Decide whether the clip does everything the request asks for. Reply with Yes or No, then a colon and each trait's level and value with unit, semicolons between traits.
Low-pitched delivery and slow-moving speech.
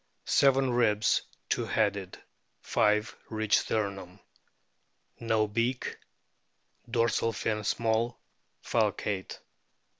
Yes: low, 110 Hz; slow, 80 wpm